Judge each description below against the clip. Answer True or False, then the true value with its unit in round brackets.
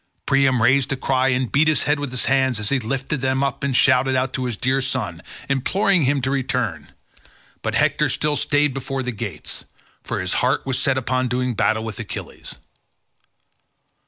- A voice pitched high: False (130 Hz)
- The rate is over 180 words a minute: True (190 wpm)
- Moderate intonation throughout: False (1.7 semitones)